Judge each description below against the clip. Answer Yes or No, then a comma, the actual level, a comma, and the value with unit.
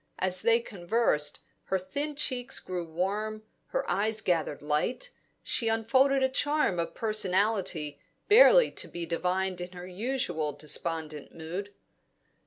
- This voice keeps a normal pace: No, slow, 130 wpm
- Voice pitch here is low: No, high, 190 Hz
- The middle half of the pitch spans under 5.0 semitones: No, wide, 5.4 semitones